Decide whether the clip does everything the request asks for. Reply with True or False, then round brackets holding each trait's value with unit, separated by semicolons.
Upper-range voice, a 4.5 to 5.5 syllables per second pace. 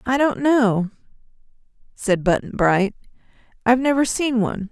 True (230 Hz; 5.0 syllables/s)